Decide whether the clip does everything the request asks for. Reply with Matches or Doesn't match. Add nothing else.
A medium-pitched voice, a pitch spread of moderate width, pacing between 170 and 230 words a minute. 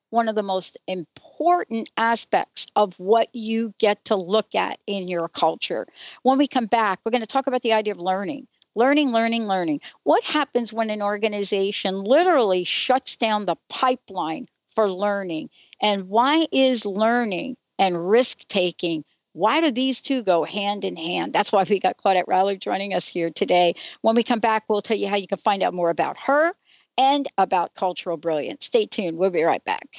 Doesn't match